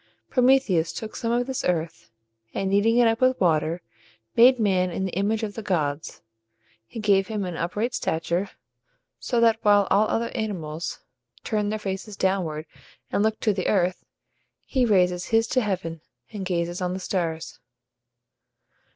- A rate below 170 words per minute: Yes, average, 160 wpm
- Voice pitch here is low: No, high, 195 Hz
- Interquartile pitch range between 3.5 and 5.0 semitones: Yes, average, 4.0 semitones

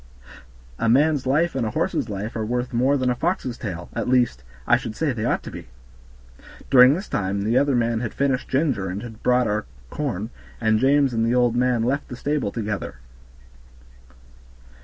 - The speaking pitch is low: Yes, low, 120 Hz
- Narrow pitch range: No, average, 3.4 semitones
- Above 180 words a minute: Yes, average, 190 wpm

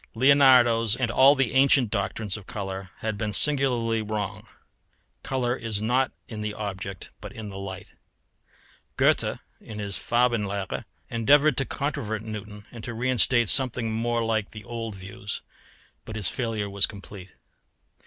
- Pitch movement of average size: Yes, average, 3.1 semitones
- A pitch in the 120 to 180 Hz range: No, low, 110 Hz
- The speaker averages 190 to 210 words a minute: No, average, 145 wpm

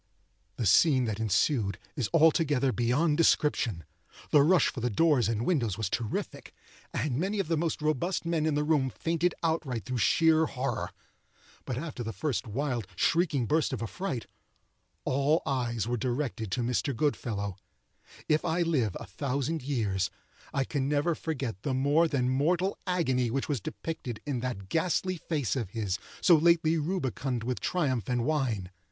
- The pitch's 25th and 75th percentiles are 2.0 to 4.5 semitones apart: No, average, 5.2 semitones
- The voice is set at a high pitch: No, low, 135 Hz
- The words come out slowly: No, average, 165 wpm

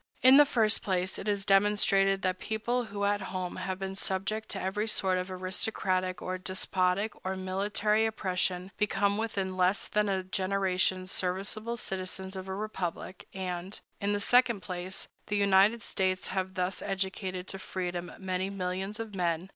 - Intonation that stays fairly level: Yes, narrow, 1.8 semitones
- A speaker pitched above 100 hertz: Yes, high, 190 Hz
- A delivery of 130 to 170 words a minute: Yes, average, 165 wpm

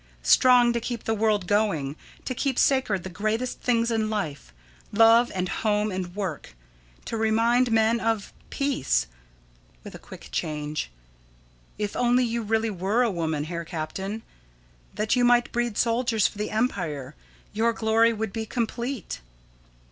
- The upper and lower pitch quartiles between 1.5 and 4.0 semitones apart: Yes, average, 3.6 semitones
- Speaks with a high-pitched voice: Yes, high, 220 Hz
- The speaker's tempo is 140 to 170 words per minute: Yes, average, 150 wpm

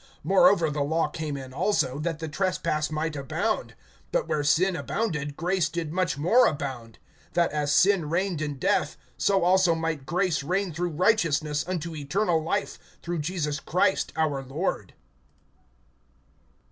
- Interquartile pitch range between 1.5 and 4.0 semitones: Yes, average, 3.7 semitones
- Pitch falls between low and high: Yes, medium, 160 Hz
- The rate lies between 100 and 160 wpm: Yes, average, 145 wpm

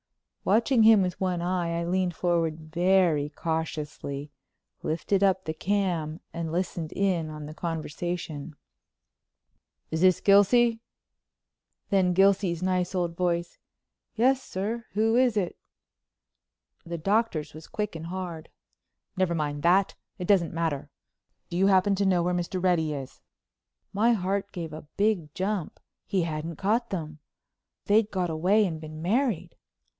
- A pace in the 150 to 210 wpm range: No, slow, 135 wpm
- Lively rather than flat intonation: No, average, 3.6 semitones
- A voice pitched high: No, medium, 180 Hz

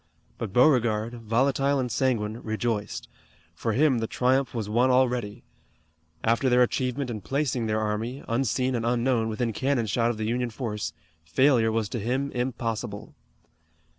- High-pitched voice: No, low, 120 Hz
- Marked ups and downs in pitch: No, average, 2.8 semitones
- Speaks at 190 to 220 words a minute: No, average, 155 wpm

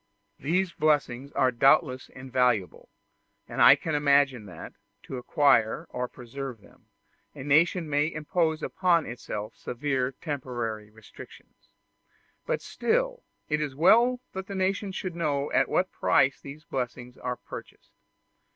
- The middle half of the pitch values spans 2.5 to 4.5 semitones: No, average, 5.0 semitones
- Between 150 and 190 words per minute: No, slow, 135 wpm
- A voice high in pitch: No, medium, 140 Hz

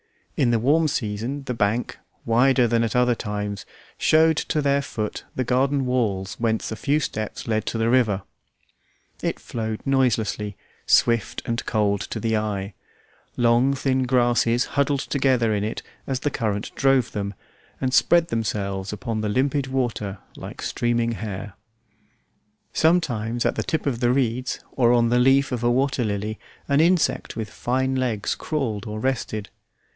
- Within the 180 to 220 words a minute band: No, average, 160 wpm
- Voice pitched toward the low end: Yes, low, 120 Hz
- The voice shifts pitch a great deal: No, average, 3.6 semitones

